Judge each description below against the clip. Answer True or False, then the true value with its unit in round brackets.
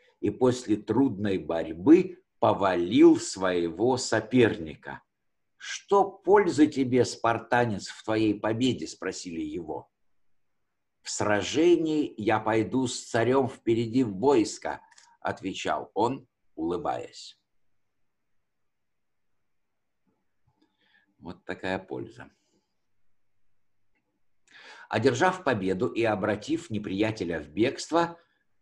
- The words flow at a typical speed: False (80 wpm)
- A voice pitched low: True (115 Hz)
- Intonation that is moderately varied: False (7.9 semitones)